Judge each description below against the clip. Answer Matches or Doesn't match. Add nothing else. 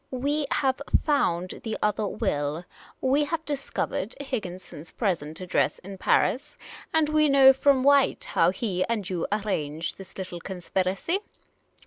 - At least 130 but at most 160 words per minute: Matches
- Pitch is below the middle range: Doesn't match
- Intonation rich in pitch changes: Matches